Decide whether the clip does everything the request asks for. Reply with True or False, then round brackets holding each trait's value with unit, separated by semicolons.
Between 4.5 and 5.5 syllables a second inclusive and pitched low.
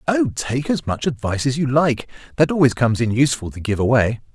False (6.1 syllables/s; 130 Hz)